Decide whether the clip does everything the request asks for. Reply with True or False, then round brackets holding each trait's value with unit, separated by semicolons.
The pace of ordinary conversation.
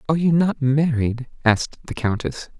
True (160 wpm)